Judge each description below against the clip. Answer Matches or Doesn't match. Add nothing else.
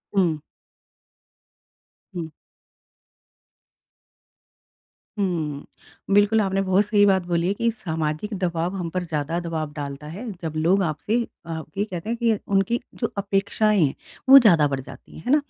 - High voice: Doesn't match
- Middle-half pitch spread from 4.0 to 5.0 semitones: Matches